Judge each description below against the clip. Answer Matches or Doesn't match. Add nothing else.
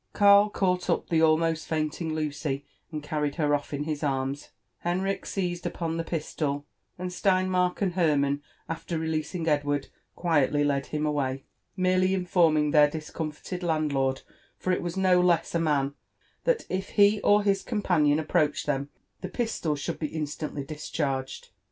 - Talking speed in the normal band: Matches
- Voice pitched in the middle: Matches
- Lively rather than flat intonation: Doesn't match